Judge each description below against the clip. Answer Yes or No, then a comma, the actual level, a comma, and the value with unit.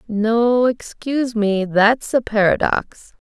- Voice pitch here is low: No, high, 225 Hz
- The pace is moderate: No, slow, 110 wpm